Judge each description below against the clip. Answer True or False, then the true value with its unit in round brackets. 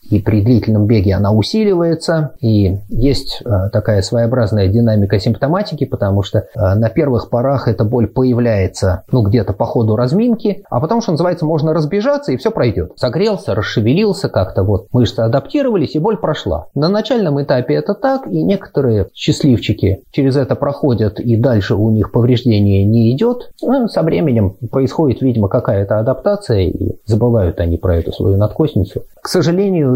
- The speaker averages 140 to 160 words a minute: True (155 wpm)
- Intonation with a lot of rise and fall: True (6.6 semitones)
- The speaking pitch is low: True (120 Hz)